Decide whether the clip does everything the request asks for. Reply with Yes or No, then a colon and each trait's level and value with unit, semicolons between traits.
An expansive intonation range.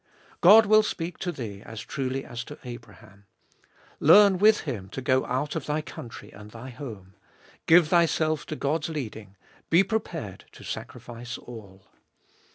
Yes: wide, 6.7 semitones